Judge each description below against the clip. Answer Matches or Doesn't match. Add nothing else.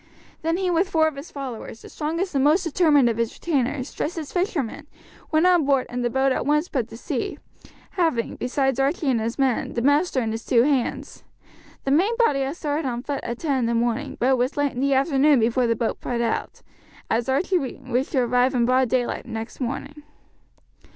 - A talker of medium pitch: Doesn't match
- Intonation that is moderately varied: Matches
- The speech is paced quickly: Matches